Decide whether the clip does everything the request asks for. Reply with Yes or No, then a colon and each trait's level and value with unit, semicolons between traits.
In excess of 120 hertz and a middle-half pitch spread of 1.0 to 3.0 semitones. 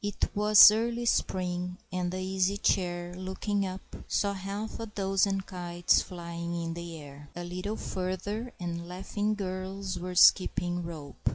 Yes: medium, 185 Hz; narrow, 2.4 semitones